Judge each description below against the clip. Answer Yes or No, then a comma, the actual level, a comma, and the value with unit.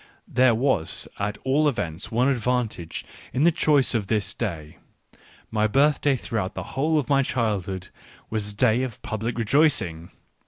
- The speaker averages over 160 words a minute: No, average, 155 wpm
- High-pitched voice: No, low, 115 Hz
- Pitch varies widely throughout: No, average, 4.7 semitones